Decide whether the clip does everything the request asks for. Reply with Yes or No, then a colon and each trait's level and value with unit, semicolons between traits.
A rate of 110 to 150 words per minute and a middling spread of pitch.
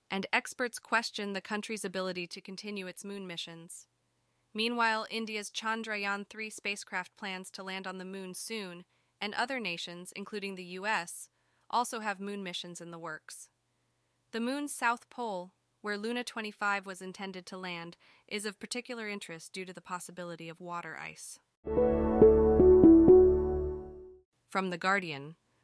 Yes: average, 145 wpm; average, 3.7 semitones